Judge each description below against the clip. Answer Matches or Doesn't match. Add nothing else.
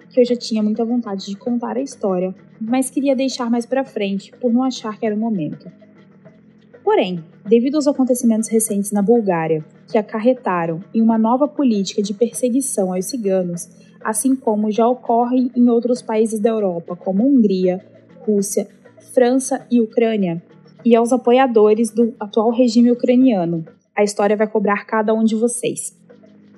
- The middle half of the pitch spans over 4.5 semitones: Doesn't match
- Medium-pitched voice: Doesn't match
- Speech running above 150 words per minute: Matches